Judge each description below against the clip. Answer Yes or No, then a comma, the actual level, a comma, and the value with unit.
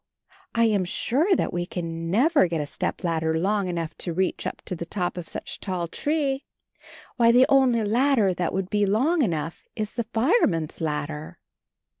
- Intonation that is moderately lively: No, wide, 6.3 semitones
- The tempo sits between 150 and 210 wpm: Yes, average, 180 wpm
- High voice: Yes, high, 195 Hz